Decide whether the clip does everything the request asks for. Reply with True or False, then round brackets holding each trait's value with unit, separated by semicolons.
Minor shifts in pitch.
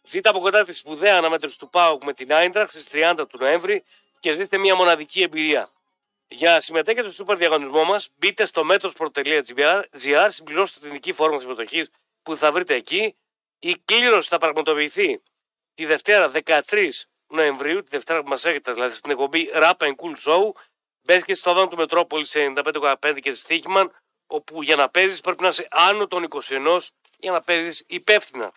False (4.2 semitones)